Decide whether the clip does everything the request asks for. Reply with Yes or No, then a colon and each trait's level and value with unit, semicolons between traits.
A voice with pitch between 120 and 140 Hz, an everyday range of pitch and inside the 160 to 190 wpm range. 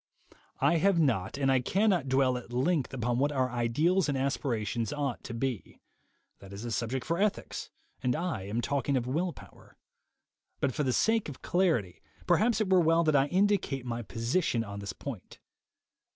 No: low, 135 Hz; wide, 6.0 semitones; average, 180 wpm